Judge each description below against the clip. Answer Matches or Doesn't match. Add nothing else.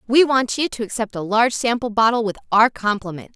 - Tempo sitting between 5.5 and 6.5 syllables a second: Matches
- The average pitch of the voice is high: Matches